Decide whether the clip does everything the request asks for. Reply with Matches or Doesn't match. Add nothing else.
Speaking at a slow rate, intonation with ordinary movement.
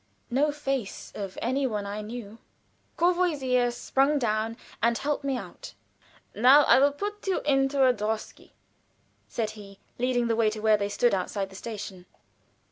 Doesn't match